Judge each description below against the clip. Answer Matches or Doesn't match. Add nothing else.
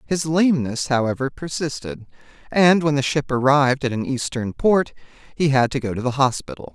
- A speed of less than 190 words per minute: Matches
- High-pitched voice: Doesn't match